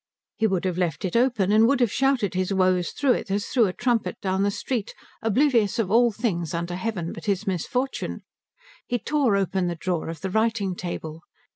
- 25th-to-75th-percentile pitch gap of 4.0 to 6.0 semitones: Yes, average, 4.3 semitones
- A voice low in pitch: No, high, 200 Hz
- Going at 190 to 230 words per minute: Yes, average, 200 wpm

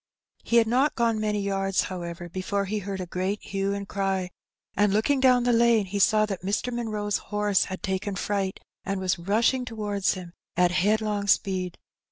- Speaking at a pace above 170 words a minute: Yes, average, 185 wpm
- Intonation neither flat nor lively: No, narrow, 2.3 semitones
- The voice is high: Yes, high, 200 Hz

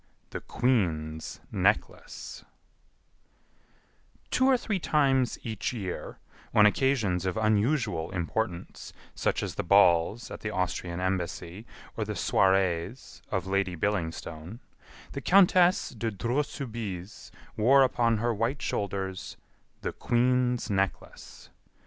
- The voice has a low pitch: Yes, low, 105 Hz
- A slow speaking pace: Yes, slow, 110 wpm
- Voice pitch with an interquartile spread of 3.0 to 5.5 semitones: Yes, average, 5.2 semitones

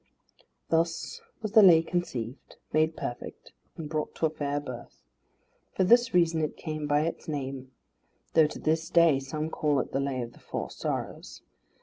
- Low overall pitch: No, medium, 155 Hz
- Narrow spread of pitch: No, average, 3.0 semitones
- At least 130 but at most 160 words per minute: No, average, 175 wpm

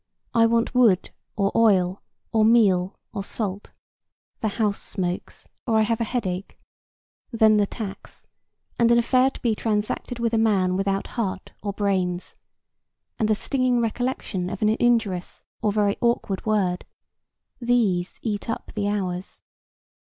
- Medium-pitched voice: No, high, 215 Hz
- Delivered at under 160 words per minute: Yes, average, 145 wpm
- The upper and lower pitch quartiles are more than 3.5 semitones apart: No, average, 3.1 semitones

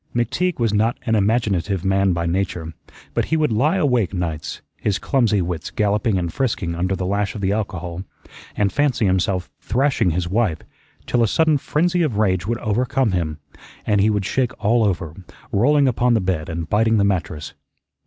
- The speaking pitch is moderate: No, low, 105 Hz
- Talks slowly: No, average, 185 wpm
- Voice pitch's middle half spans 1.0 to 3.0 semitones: No, average, 4.6 semitones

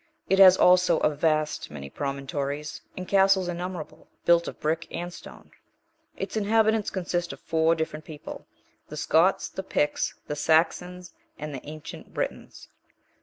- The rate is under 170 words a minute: Yes, average, 145 wpm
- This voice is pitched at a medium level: Yes, medium, 165 Hz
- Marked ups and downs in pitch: No, average, 3.1 semitones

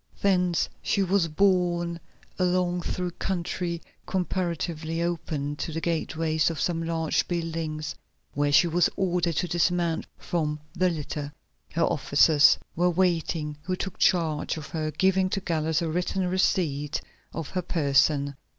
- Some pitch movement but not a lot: No, narrow, 2.3 semitones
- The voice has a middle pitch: Yes, medium, 170 Hz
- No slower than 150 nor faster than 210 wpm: No, average, 140 wpm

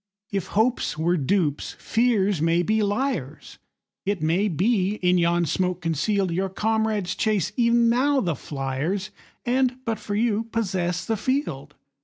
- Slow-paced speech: Yes, slow, 130 wpm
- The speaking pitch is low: No, high, 200 Hz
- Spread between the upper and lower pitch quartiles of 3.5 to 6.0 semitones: Yes, average, 4.5 semitones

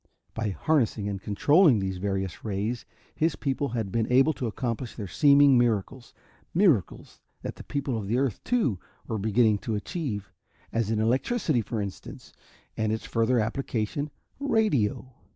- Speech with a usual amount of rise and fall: Yes, average, 4.8 semitones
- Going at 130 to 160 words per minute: Yes, average, 150 wpm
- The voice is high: No, low, 115 Hz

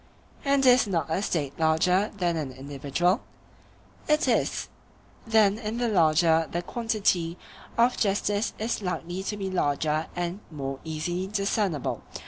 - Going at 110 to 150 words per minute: Yes, slow, 135 wpm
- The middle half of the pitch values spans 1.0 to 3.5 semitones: No, average, 4.8 semitones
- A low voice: No, medium, 180 Hz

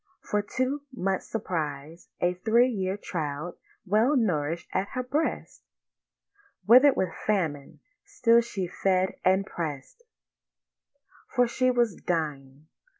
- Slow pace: Yes, slow, 115 wpm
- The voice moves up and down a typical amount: No, wide, 6.3 semitones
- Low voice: No, high, 190 Hz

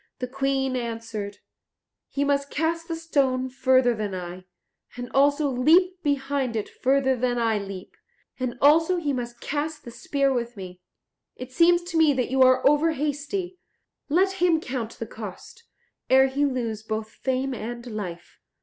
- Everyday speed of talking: Yes, average, 160 wpm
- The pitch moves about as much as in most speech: Yes, average, 3.8 semitones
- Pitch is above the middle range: Yes, very high, 260 Hz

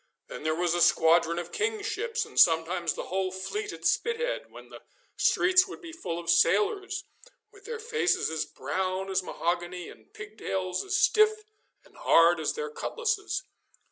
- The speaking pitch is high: Yes, very high, 335 Hz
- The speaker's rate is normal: Yes, average, 170 wpm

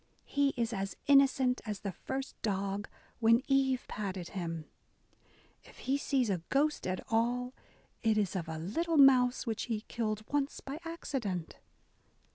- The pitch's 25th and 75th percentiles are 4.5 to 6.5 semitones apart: Yes, wide, 5.4 semitones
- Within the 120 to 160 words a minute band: Yes, average, 150 wpm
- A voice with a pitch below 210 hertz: No, high, 230 Hz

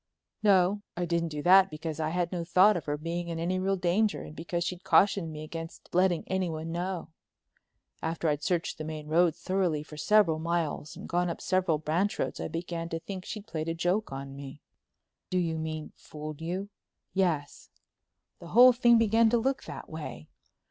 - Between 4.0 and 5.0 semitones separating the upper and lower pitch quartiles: No, average, 3.1 semitones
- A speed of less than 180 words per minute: No, average, 190 wpm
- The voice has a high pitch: No, medium, 170 Hz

